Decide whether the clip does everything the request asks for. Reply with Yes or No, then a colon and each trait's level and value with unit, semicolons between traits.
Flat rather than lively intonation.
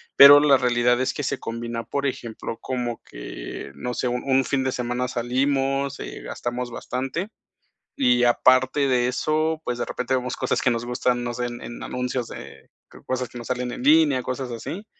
Yes: narrow, 1.7 semitones